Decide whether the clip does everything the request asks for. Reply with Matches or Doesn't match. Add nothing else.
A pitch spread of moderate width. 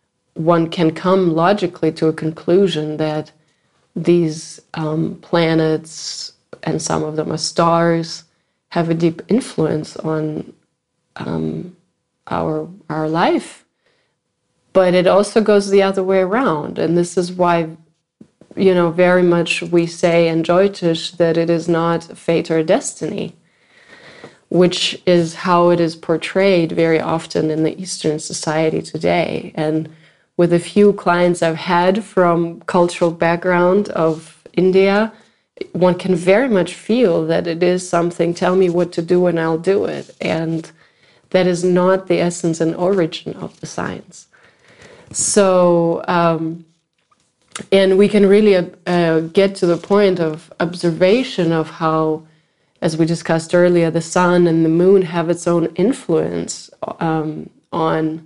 Doesn't match